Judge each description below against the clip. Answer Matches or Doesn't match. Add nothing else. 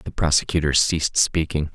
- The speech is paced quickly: Doesn't match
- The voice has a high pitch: Doesn't match